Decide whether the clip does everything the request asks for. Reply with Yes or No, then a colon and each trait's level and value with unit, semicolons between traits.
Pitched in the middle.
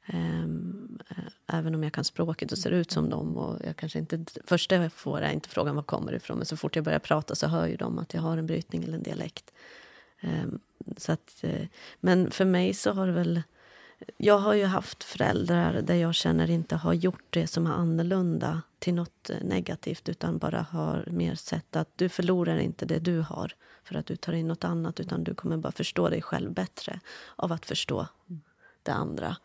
Yes: medium, 165 Hz